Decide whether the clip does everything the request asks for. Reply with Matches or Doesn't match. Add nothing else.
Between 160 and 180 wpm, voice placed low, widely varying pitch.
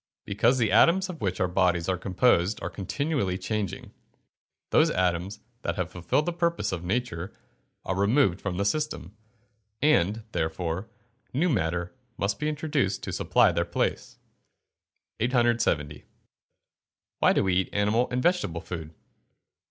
Doesn't match